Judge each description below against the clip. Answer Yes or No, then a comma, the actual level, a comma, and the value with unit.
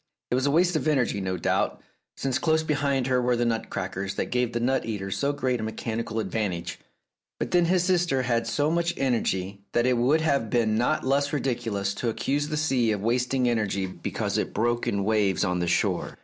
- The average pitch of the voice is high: No, low, 120 Hz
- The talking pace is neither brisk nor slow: No, fast, 210 wpm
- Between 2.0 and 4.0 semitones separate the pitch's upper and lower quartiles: No, average, 4.6 semitones